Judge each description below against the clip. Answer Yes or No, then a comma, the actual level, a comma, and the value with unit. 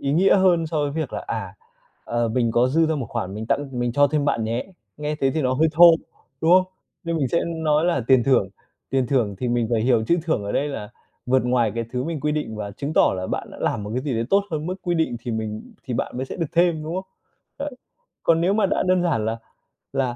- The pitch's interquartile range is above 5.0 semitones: Yes, wide, 5.5 semitones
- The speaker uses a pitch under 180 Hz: Yes, medium, 140 Hz